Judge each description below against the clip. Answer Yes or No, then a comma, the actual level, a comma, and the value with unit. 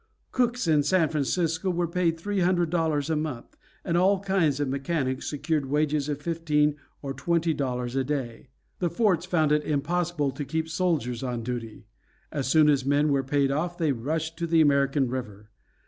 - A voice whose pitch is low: No, medium, 150 Hz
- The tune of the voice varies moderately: Yes, average, 3.6 semitones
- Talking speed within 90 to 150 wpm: No, average, 180 wpm